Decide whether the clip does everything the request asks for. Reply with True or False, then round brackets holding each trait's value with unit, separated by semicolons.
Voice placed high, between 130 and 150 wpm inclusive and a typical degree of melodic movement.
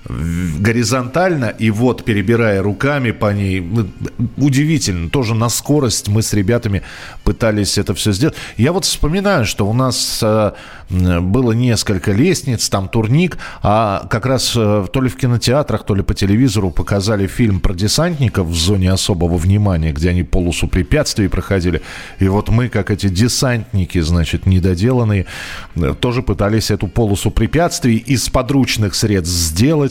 False (105 Hz; 140 wpm; 4.4 semitones)